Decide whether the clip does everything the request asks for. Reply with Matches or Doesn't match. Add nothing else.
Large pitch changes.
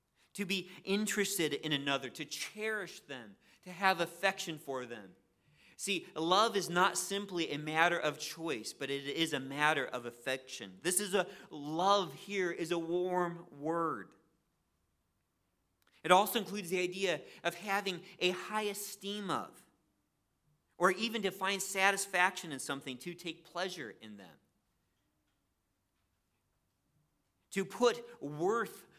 Matches